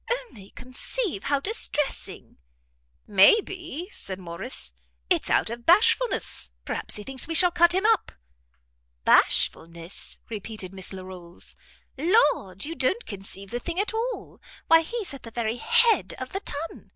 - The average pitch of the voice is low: No, very high, 275 Hz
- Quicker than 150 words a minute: No, average, 145 wpm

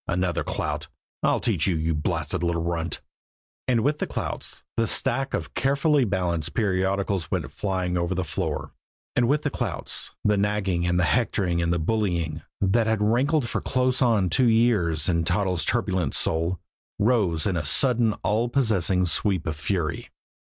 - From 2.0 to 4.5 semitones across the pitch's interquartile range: No, average, 5.1 semitones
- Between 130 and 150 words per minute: No, average, 165 wpm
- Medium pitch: No, very low, 95 Hz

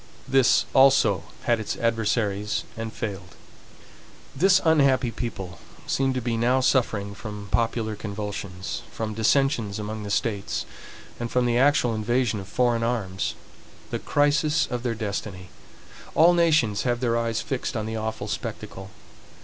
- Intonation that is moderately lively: Yes, average, 3.6 semitones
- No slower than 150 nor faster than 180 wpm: No, average, 140 wpm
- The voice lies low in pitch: Yes, low, 115 Hz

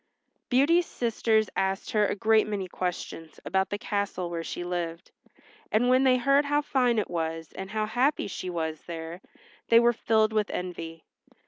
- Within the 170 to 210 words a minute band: Yes, average, 175 wpm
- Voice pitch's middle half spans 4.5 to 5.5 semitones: Yes, average, 5.2 semitones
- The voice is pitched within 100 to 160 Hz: No, high, 205 Hz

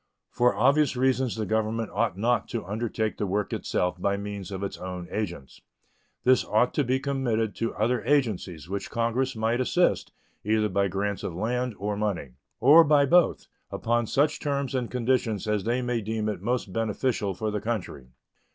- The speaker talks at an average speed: Yes, average, 175 wpm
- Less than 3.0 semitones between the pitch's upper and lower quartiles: No, average, 3.6 semitones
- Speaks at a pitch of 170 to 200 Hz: No, low, 110 Hz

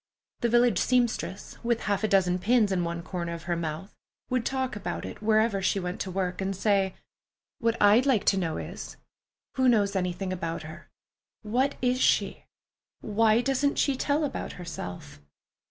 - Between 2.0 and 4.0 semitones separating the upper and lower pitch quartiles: No, average, 4.9 semitones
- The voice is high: Yes, high, 200 Hz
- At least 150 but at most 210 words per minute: Yes, average, 170 wpm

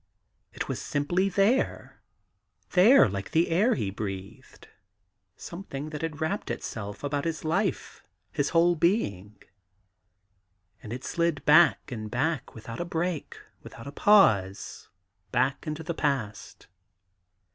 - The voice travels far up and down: Yes, wide, 7.5 semitones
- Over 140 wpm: No, slow, 135 wpm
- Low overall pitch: No, medium, 150 Hz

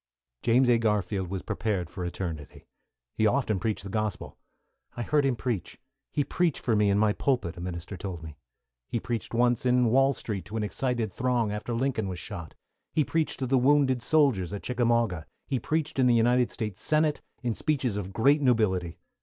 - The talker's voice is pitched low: Yes, low, 115 Hz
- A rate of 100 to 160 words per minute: No, average, 190 wpm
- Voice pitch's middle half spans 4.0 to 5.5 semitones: Yes, average, 4.6 semitones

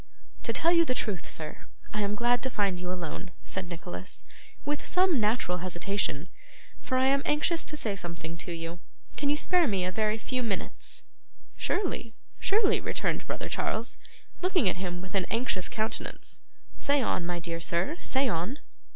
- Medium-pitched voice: No, high, 210 Hz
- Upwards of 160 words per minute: Yes, average, 175 wpm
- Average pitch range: No, wide, 7.1 semitones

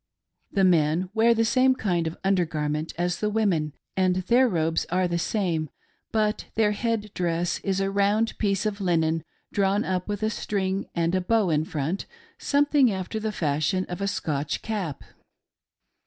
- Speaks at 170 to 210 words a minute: Yes, average, 175 wpm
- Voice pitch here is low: No, high, 190 Hz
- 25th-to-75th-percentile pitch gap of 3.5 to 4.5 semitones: Yes, average, 4.0 semitones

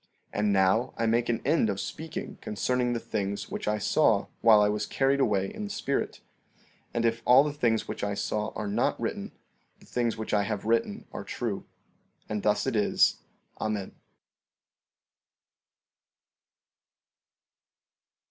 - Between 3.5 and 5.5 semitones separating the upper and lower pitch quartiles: No, average, 2.8 semitones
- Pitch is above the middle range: No, low, 110 Hz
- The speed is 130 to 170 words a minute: Yes, average, 155 wpm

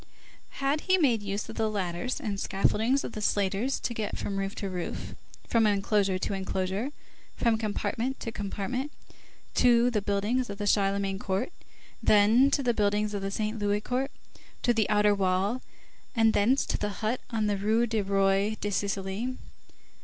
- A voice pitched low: No, high, 210 Hz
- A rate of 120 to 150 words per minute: No, average, 175 wpm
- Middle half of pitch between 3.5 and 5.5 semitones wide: No, average, 2.9 semitones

